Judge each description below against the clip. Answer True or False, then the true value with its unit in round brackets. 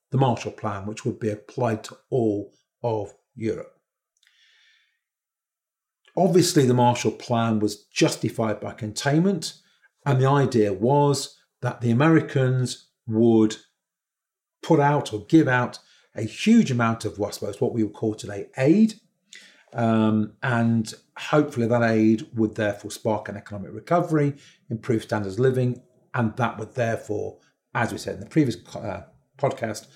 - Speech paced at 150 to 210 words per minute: False (140 wpm)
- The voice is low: True (120 Hz)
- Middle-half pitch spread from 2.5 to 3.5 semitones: False (4.7 semitones)